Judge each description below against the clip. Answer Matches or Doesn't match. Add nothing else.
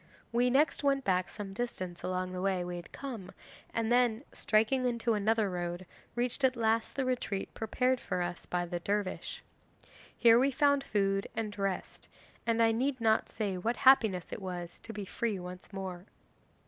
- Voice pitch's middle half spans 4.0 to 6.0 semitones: Matches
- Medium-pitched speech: Doesn't match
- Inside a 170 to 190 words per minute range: Matches